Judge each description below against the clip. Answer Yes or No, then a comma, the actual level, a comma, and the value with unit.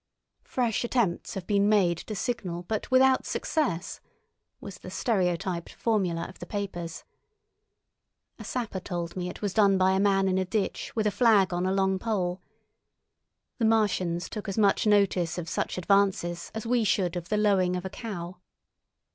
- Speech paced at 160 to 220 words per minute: Yes, average, 170 wpm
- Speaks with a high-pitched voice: Yes, high, 195 Hz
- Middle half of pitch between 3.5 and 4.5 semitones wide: No, average, 3.1 semitones